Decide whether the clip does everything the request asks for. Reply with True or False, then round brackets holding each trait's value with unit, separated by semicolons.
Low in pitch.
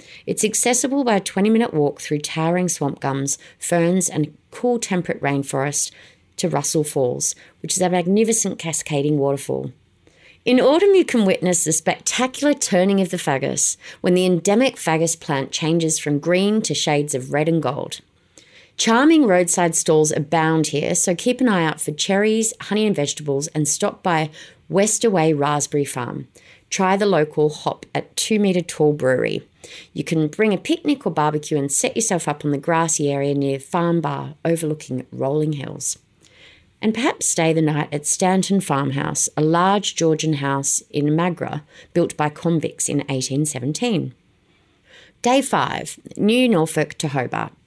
False (165 Hz)